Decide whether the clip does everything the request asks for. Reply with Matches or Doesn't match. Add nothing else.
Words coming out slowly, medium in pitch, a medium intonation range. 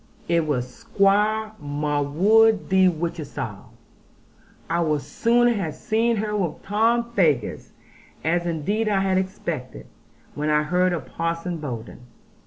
Doesn't match